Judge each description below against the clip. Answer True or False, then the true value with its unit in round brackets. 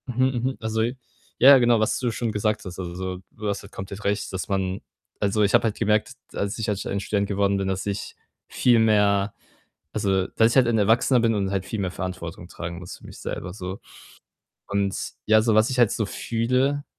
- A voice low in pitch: True (105 Hz)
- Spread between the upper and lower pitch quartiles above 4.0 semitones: False (2.8 semitones)